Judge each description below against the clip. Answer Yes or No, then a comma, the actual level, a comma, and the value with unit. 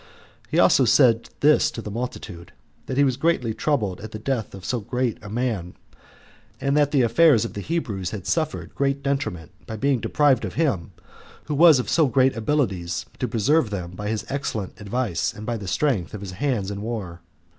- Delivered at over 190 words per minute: Yes, average, 200 wpm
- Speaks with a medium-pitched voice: No, low, 115 Hz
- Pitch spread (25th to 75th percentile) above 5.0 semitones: Yes, wide, 5.6 semitones